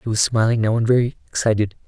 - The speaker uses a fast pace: Yes, fast, 225 wpm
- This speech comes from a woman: No, male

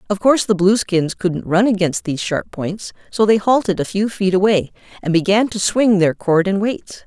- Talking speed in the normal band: No, fast, 210 wpm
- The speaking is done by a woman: Yes, female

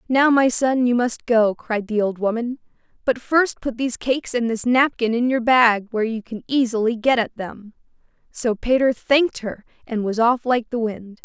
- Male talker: No, female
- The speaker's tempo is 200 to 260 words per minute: Yes, fast, 205 wpm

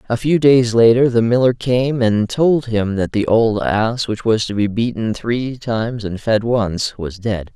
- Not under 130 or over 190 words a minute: No, fast, 205 wpm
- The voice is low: Yes, low, 115 Hz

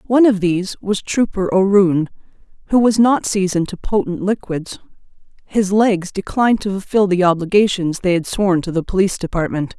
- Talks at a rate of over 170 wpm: No, average, 165 wpm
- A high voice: Yes, high, 195 Hz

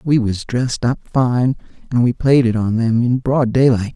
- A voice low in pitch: Yes, low, 120 Hz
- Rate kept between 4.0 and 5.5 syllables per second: Yes, 4.8 syllables/s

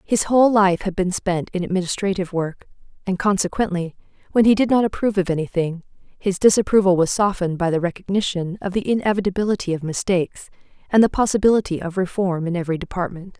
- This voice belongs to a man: No, female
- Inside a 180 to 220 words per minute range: No, average, 170 wpm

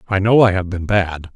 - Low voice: Yes, very low, 95 Hz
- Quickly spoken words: Yes, fast, 265 wpm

